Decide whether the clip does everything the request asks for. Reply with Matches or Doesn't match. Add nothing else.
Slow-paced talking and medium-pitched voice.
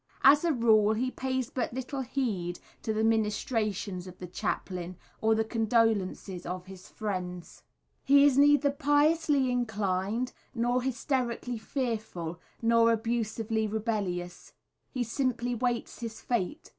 Doesn't match